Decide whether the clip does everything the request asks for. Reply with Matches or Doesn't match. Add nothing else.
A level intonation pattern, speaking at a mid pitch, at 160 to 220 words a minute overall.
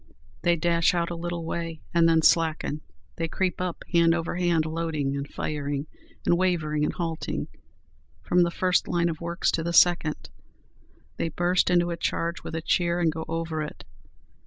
Matches